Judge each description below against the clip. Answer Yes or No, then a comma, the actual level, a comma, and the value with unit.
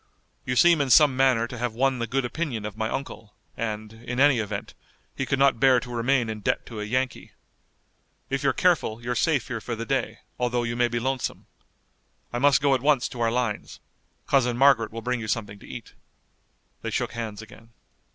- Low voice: Yes, low, 120 Hz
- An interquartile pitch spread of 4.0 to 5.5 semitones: No, average, 2.8 semitones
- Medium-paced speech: No, fast, 210 wpm